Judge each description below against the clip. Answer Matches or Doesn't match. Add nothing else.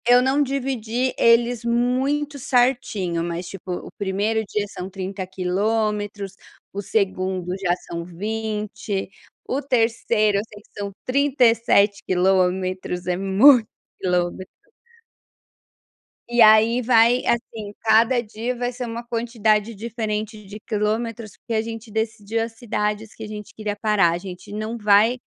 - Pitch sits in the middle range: Doesn't match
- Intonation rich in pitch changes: Doesn't match